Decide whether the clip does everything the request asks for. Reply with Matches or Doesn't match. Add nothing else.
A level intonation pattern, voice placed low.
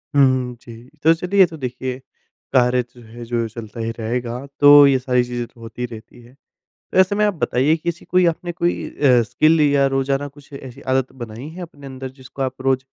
Doesn't match